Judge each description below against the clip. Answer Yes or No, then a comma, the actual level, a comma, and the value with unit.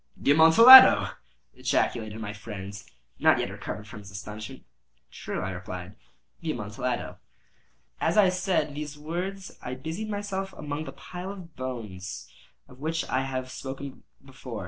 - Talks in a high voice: No, medium, 140 Hz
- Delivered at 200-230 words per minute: No, average, 145 wpm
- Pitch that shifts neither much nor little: No, wide, 8.5 semitones